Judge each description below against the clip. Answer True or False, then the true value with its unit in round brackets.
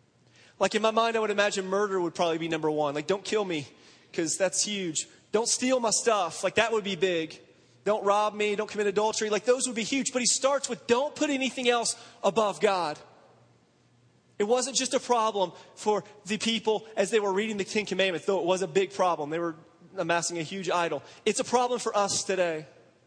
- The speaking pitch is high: True (205 Hz)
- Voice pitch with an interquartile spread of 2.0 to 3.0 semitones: False (3.8 semitones)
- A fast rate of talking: True (215 wpm)